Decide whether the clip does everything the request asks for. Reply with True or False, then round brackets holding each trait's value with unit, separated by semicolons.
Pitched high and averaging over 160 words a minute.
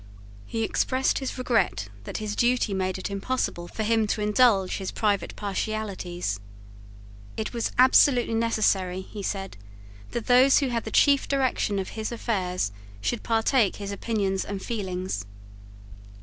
False (215 Hz; 145 wpm)